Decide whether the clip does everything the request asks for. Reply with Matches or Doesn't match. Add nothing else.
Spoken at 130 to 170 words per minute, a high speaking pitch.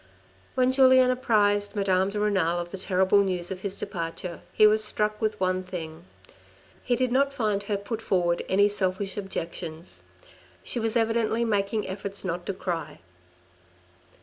Matches